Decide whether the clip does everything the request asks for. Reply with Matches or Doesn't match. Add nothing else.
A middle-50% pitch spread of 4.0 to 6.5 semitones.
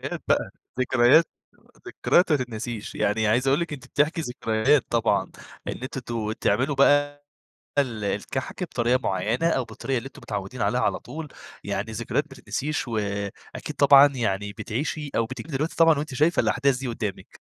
Matches